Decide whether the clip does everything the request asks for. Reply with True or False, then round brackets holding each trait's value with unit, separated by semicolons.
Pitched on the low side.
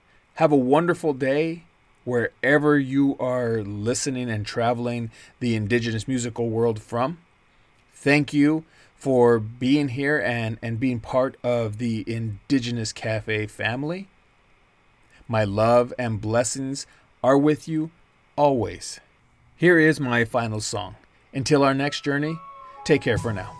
True (125 Hz)